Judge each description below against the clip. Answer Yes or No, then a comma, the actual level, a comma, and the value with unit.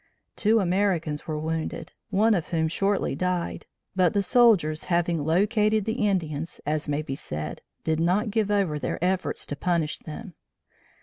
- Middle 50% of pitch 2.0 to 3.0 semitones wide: No, average, 4.5 semitones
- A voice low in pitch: No, medium, 175 Hz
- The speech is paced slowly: No, average, 160 wpm